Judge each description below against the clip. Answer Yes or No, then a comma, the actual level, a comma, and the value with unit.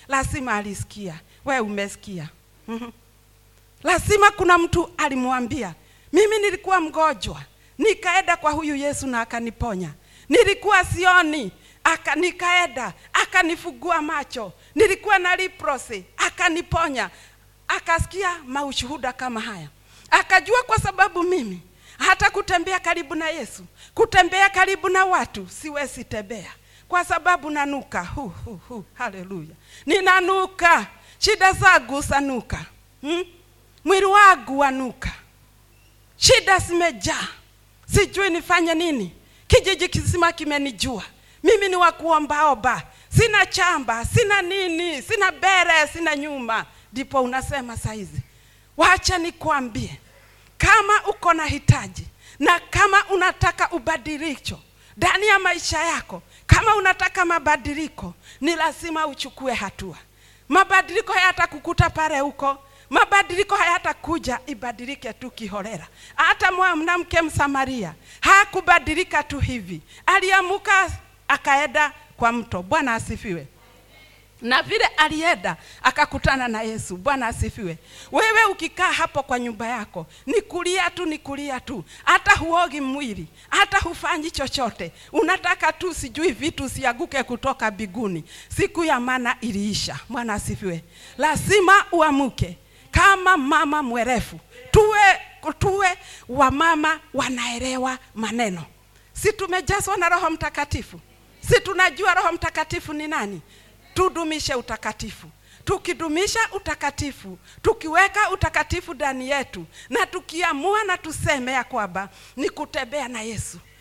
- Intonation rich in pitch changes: Yes, wide, 6.4 semitones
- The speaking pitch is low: No, very high, 315 Hz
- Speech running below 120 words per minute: Yes, slow, 100 wpm